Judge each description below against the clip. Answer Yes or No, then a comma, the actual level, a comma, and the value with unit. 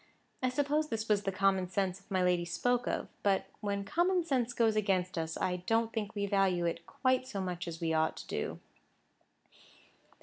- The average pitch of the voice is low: No, high, 200 Hz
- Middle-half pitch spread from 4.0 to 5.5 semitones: Yes, average, 4.3 semitones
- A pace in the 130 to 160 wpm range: No, average, 190 wpm